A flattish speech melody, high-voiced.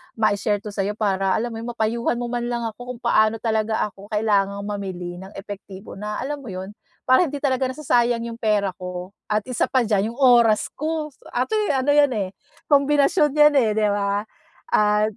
No: average, 3.7 semitones; high, 220 Hz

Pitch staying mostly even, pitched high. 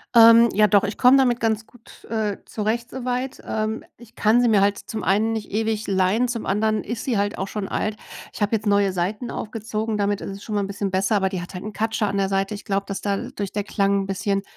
Yes: narrow, 2.1 semitones; high, 210 Hz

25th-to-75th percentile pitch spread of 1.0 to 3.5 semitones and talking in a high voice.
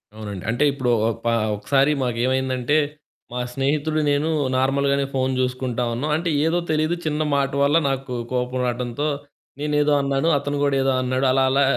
No: narrow, 2.5 semitones; low, 135 Hz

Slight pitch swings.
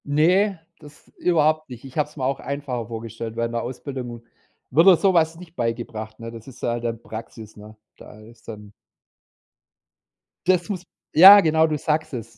No: wide, 5.6 semitones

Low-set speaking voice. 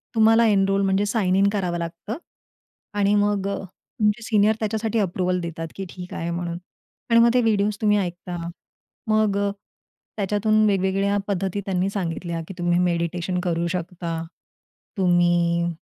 No: high, 195 Hz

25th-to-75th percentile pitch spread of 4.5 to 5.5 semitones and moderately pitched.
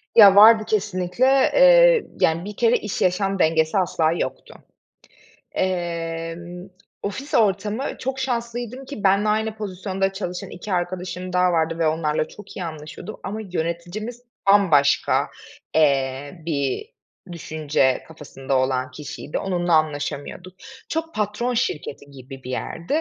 Yes: average, 5.0 semitones; medium, 180 Hz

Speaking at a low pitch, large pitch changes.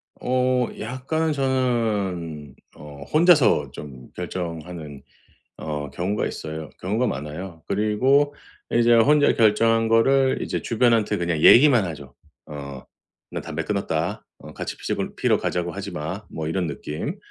Yes: low, 100 Hz; wide, 7.8 semitones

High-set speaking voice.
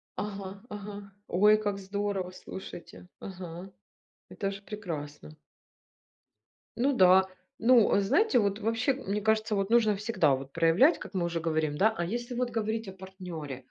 Yes: high, 200 Hz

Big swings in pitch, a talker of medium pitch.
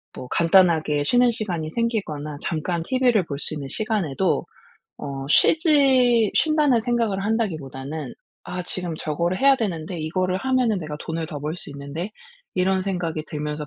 Yes: wide, 6.4 semitones; medium, 180 Hz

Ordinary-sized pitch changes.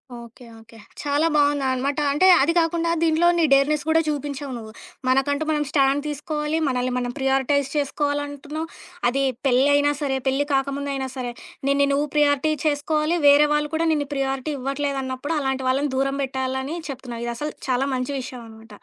No: narrow, 2.1 semitones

